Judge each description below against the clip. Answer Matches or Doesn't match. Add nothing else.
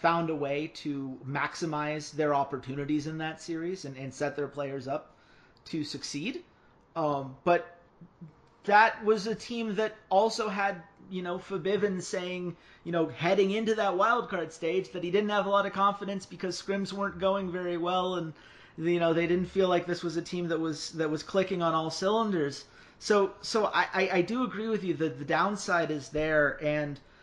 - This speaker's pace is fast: Doesn't match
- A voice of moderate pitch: Matches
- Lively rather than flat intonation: Doesn't match